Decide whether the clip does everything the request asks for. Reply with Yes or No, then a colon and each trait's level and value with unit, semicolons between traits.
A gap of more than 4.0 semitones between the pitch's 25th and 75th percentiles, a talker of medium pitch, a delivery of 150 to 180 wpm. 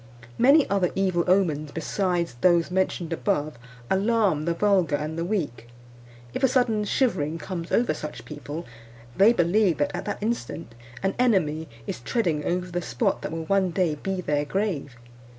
Yes: average, 4.4 semitones; medium, 175 Hz; average, 165 wpm